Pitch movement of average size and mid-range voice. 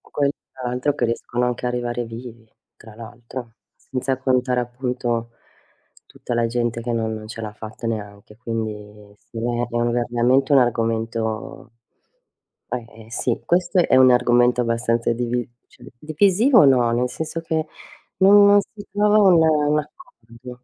No: average, 3.0 semitones; low, 120 Hz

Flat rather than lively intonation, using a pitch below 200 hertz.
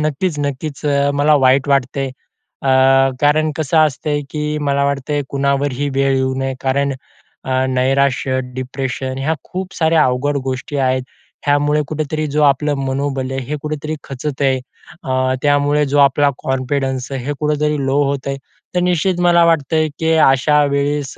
Yes: narrow, 2.1 semitones; medium, 140 Hz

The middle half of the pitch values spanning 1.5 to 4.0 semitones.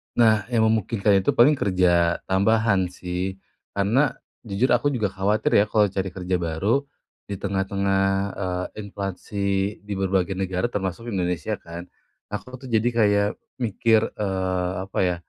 Yes: average, 2.8 semitones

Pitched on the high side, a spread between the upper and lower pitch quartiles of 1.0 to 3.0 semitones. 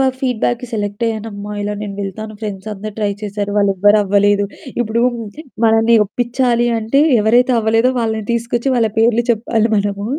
Yes: high, 220 Hz; narrow, 2.4 semitones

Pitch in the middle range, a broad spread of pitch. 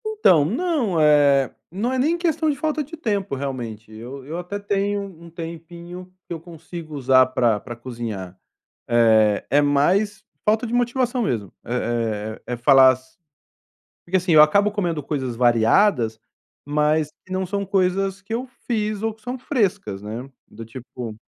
Yes: medium, 165 Hz; wide, 8.5 semitones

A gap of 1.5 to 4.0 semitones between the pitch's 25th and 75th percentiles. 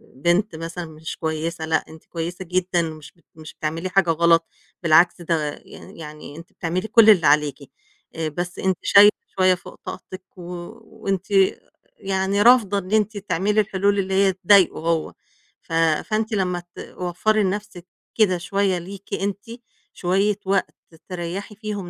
Yes: average, 3.2 semitones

